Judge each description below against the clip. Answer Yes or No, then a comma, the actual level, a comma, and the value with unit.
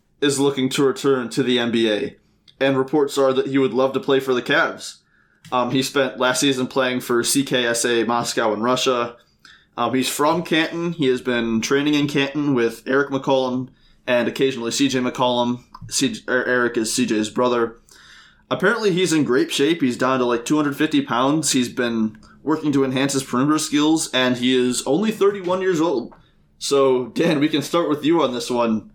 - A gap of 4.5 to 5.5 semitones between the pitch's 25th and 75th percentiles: No, average, 2.7 semitones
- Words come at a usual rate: Yes, average, 180 wpm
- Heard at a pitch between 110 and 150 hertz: Yes, low, 130 Hz